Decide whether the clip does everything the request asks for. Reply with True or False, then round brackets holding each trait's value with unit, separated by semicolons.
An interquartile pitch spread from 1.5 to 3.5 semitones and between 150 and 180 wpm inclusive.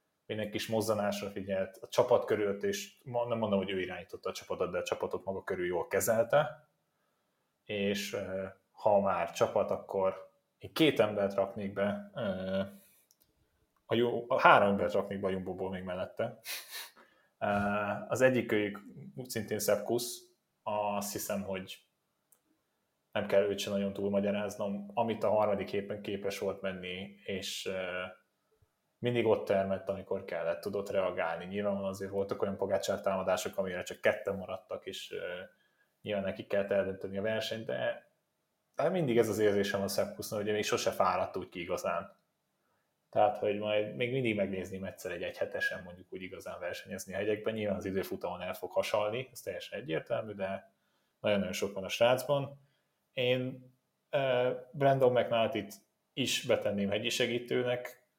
False (3.9 semitones; 155 wpm)